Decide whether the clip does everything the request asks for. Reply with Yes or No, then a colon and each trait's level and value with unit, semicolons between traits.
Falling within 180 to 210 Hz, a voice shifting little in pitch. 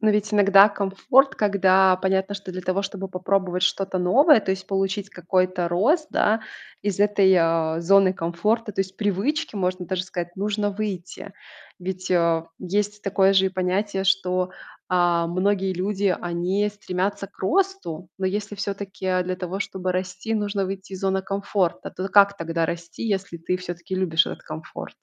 Yes: high, 190 Hz; narrow, 1.8 semitones